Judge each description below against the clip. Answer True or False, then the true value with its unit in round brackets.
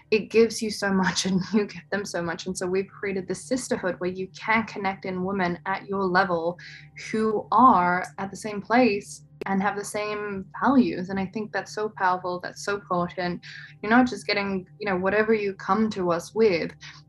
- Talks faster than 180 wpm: True (205 wpm)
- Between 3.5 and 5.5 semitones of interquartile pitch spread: False (2.7 semitones)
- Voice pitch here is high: True (195 Hz)